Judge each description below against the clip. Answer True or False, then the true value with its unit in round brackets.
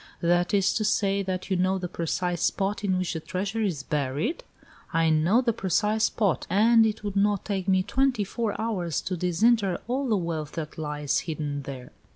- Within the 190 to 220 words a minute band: True (195 wpm)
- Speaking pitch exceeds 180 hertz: True (190 Hz)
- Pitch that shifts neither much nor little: True (4.2 semitones)